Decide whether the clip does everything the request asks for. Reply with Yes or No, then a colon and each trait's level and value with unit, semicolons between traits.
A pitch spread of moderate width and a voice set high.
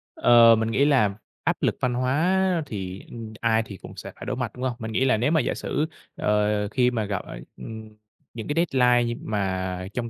No: average, 3.3 semitones; low, 115 Hz